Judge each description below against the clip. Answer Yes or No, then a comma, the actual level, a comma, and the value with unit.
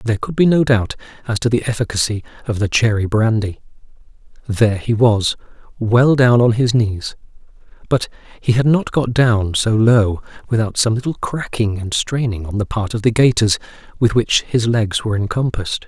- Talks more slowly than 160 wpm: No, average, 180 wpm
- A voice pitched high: No, low, 115 Hz